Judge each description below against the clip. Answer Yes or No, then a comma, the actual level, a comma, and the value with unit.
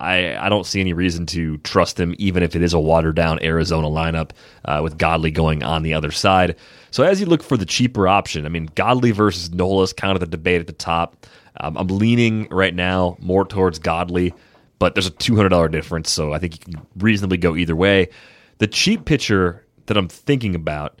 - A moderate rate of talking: No, fast, 215 wpm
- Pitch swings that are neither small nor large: Yes, average, 3.3 semitones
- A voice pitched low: Yes, very low, 90 Hz